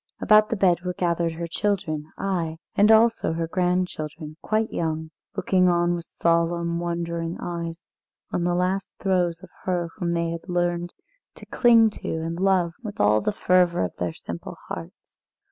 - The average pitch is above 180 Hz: No, medium, 175 Hz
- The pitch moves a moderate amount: No, narrow, 1.9 semitones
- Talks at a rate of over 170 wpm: No, average, 165 wpm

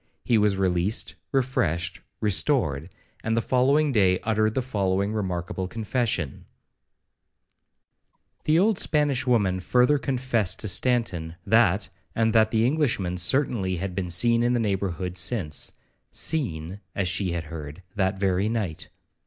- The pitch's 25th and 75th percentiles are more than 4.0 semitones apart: Yes, average, 5.1 semitones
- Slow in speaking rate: Yes, slow, 130 wpm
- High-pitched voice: No, low, 105 Hz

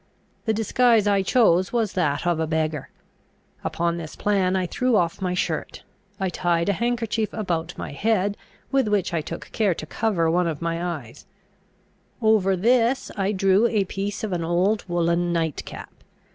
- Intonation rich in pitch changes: No, average, 4.1 semitones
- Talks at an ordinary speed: Yes, average, 170 wpm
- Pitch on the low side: No, medium, 185 Hz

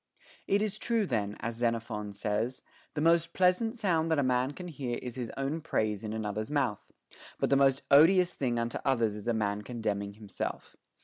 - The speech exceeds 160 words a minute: Yes, average, 190 wpm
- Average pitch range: No, wide, 6.7 semitones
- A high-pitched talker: No, low, 125 Hz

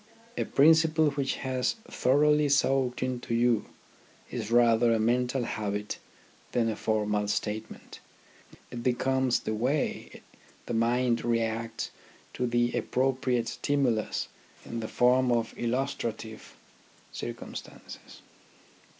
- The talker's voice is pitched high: No, low, 120 Hz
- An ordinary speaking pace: No, slow, 110 wpm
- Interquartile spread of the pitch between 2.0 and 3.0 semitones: Yes, narrow, 2.5 semitones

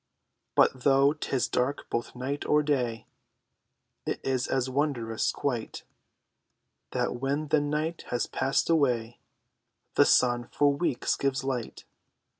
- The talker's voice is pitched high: No, low, 135 Hz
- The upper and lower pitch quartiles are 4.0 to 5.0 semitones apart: No, average, 2.8 semitones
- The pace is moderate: No, slow, 125 wpm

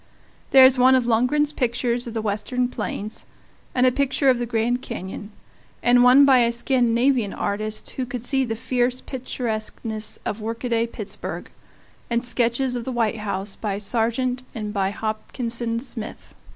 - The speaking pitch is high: Yes, high, 235 Hz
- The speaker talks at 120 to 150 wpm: No, average, 160 wpm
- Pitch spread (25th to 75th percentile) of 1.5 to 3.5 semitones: Yes, narrow, 2.5 semitones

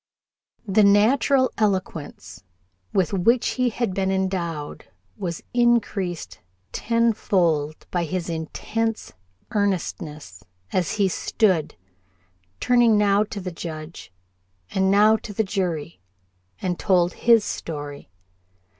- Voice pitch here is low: No, high, 190 Hz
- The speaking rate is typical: No, slow, 105 wpm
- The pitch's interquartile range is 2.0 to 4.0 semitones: No, average, 4.5 semitones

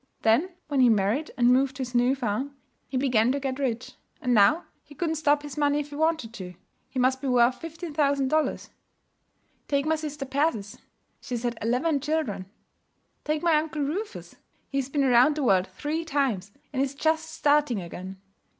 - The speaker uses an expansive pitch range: No, average, 3.8 semitones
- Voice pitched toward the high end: Yes, very high, 275 Hz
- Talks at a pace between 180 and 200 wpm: Yes, average, 185 wpm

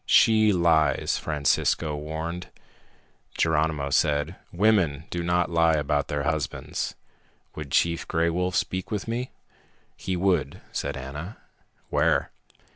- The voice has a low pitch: Yes, very low, 80 Hz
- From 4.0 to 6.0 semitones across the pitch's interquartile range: No, average, 3.2 semitones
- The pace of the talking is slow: Yes, slow, 120 wpm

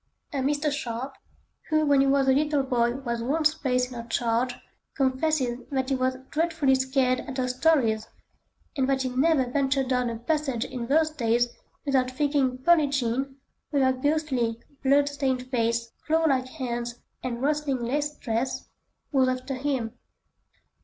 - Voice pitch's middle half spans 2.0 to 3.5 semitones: Yes, narrow, 2.5 semitones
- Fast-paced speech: No, average, 160 wpm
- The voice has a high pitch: Yes, very high, 265 Hz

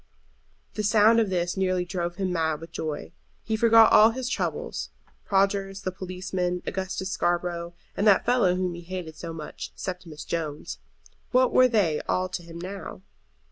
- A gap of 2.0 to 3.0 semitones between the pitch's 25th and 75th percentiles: Yes, narrow, 2.6 semitones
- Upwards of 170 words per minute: No, average, 165 wpm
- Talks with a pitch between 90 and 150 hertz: No, medium, 185 Hz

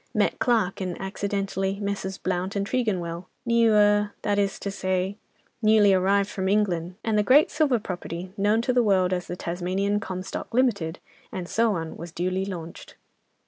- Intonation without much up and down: Yes, narrow, 2.3 semitones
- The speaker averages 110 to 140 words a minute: No, average, 160 wpm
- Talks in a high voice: Yes, high, 195 Hz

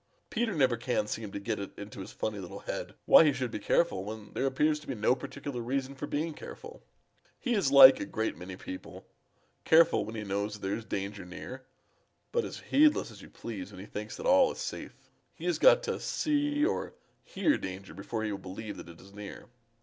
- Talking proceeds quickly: Yes, fast, 220 wpm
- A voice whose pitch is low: Yes, low, 115 Hz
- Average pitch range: No, wide, 7.1 semitones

